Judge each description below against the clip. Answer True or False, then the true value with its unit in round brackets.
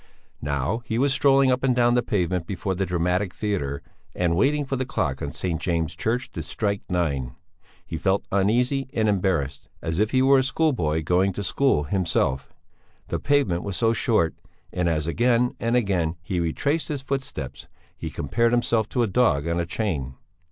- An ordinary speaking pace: True (185 wpm)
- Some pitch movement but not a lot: False (6.7 semitones)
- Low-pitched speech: True (100 Hz)